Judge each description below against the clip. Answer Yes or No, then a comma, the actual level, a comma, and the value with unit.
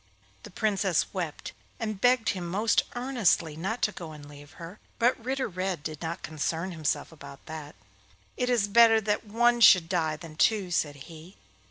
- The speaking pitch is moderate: Yes, medium, 180 Hz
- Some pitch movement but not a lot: No, wide, 5.8 semitones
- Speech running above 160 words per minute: Yes, average, 175 wpm